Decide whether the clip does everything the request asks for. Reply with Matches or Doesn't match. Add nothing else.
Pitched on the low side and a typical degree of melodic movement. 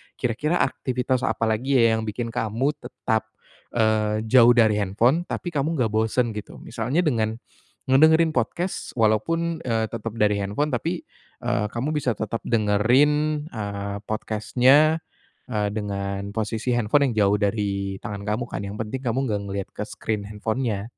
Matches